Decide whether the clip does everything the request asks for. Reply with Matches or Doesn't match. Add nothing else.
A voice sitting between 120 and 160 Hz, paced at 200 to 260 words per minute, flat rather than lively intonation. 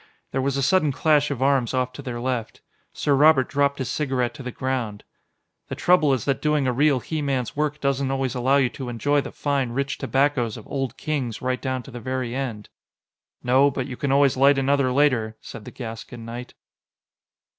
Matches